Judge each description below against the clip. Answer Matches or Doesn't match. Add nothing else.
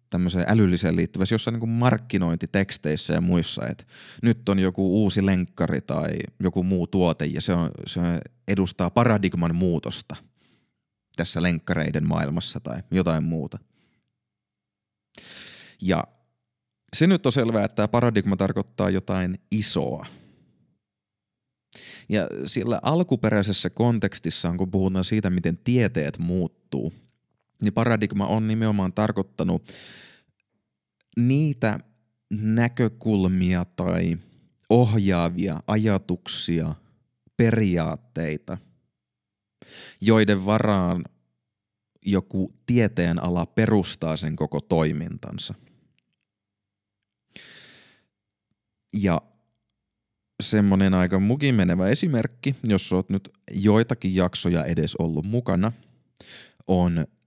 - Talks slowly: Matches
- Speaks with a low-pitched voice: Matches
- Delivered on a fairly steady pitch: Doesn't match